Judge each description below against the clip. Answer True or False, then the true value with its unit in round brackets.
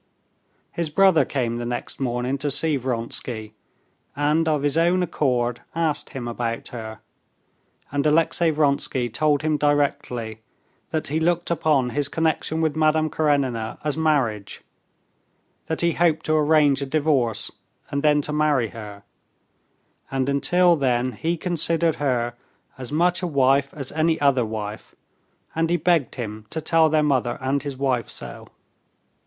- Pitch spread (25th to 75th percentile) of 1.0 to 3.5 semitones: False (4.3 semitones)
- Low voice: False (145 Hz)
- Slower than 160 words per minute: True (150 wpm)